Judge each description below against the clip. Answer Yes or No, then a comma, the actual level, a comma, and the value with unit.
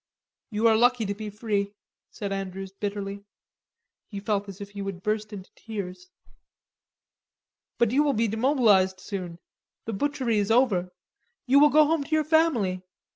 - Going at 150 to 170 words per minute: Yes, average, 160 wpm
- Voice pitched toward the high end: Yes, high, 210 Hz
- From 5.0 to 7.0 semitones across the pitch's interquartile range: No, average, 3.9 semitones